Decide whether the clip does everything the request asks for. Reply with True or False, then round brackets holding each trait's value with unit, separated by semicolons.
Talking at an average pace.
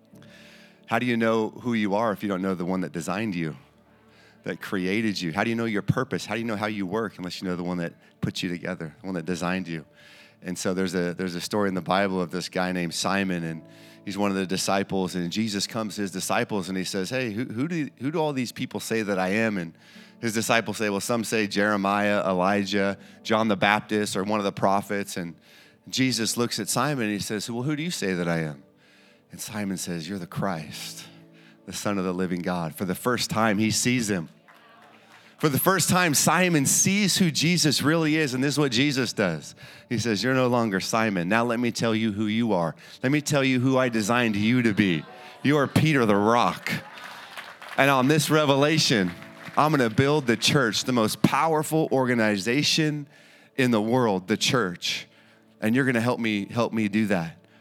False (225 wpm)